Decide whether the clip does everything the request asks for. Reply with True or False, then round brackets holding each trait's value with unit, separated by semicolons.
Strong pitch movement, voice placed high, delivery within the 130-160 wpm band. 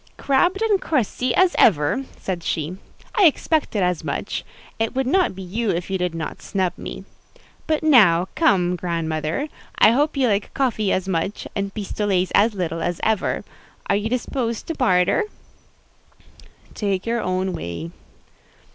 True (6.2 semitones; 200 Hz; 155 wpm)